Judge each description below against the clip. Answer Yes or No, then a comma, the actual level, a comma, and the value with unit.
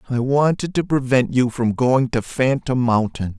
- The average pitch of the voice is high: No, low, 125 Hz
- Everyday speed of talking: Yes, average, 175 wpm